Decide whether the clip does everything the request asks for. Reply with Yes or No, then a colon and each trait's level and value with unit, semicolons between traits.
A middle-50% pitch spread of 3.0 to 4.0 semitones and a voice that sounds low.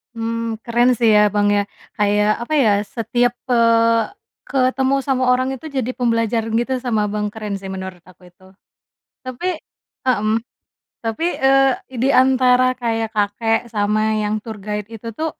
No: average, 3.3 semitones; high, 230 Hz